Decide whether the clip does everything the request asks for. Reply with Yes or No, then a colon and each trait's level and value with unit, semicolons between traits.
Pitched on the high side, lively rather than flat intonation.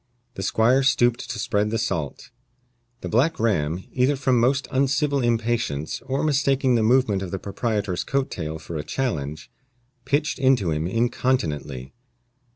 No: low, 115 Hz; wide, 7.0 semitones